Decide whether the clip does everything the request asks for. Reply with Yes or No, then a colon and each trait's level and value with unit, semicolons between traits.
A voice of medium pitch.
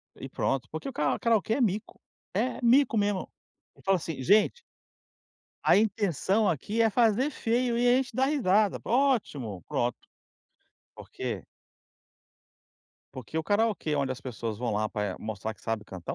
No: high, 200 Hz